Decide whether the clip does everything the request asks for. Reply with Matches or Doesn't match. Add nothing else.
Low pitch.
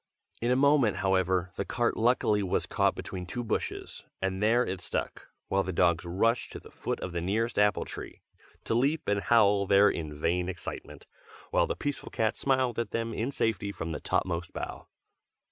Matches